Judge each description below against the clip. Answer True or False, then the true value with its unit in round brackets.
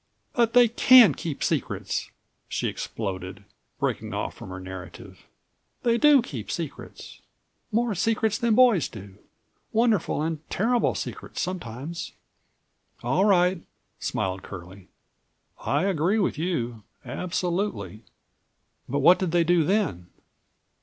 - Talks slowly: True (115 wpm)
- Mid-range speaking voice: True (175 Hz)